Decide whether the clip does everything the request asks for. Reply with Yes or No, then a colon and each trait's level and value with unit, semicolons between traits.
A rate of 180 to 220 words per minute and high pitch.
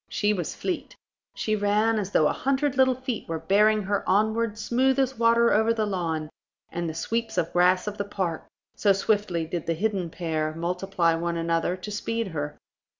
Yes: average, 190 wpm; high, 200 Hz